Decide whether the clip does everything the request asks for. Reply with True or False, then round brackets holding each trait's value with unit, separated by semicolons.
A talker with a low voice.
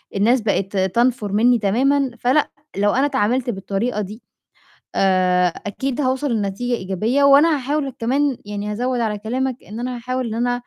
False (240 Hz)